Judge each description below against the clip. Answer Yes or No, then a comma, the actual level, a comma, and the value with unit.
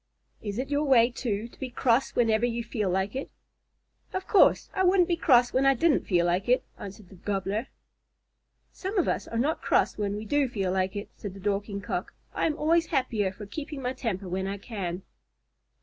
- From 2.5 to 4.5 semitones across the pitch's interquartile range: No, wide, 5.4 semitones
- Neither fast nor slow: No, fast, 210 wpm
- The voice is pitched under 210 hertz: No, high, 230 Hz